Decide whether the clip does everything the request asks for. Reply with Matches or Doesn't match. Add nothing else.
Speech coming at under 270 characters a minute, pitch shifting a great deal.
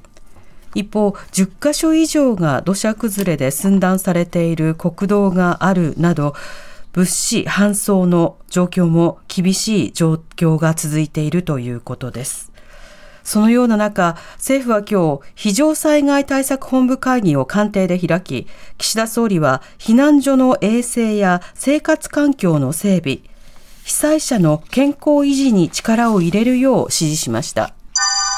Matches